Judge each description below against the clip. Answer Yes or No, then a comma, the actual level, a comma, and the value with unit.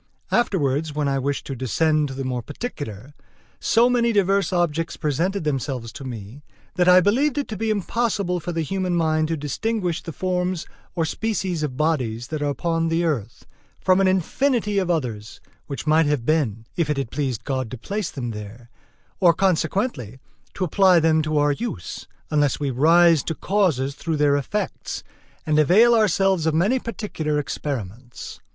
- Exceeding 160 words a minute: Yes, average, 175 wpm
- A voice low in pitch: No, medium, 160 Hz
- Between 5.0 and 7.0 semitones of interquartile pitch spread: Yes, average, 5.3 semitones